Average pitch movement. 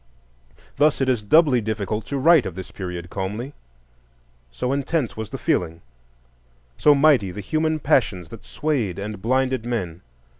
No: wide, 6.5 semitones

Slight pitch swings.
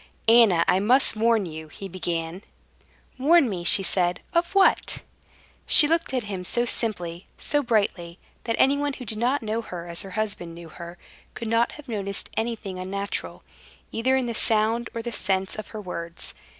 No: average, 4.8 semitones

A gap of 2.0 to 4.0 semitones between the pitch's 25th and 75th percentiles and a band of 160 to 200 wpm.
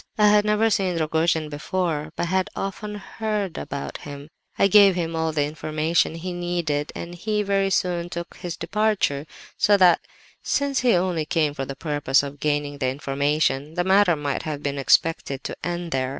No: average, 4.5 semitones; average, 180 wpm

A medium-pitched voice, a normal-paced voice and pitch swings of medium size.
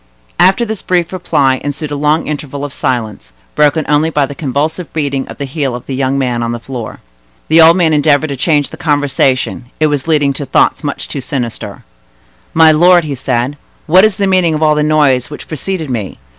No: medium, 145 Hz; fast, 210 wpm; average, 3.2 semitones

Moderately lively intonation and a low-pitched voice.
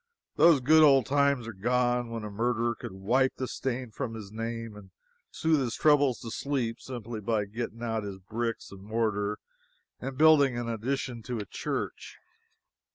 Yes: average, 3.2 semitones; low, 120 Hz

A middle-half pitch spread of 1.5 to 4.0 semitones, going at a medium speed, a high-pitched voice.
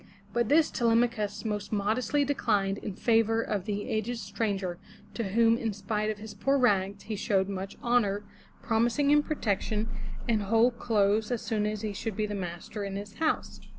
Yes: narrow, 2.5 semitones; average, 185 wpm; high, 215 Hz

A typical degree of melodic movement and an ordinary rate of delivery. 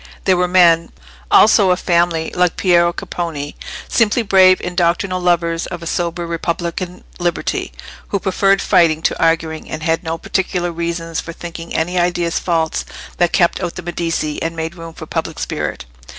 No: narrow, 1.4 semitones; average, 165 wpm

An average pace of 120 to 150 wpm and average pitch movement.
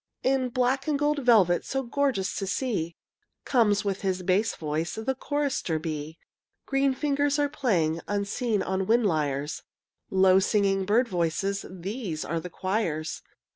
No: average, 140 wpm; wide, 6.6 semitones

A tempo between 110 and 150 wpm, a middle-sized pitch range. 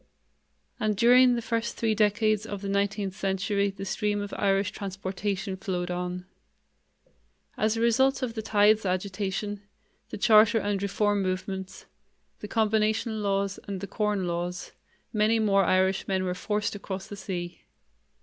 No: average, 145 wpm; narrow, 2.0 semitones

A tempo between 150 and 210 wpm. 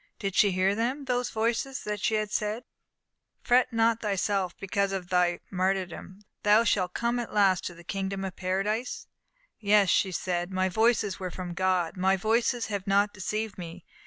Yes: average, 170 wpm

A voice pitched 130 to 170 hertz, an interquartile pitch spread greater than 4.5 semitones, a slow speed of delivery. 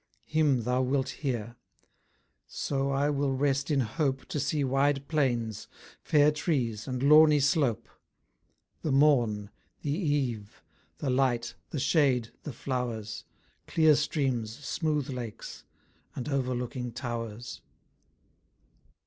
No: low, 135 Hz; average, 3.2 semitones; slow, 115 wpm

